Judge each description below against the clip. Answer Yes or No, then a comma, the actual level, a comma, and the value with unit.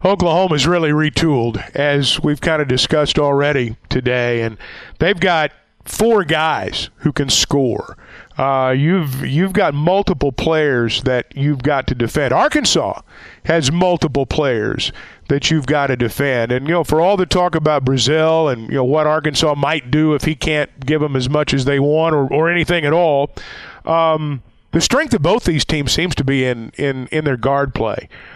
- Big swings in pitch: No, average, 3.2 semitones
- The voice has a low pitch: No, medium, 150 Hz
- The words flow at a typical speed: Yes, average, 180 wpm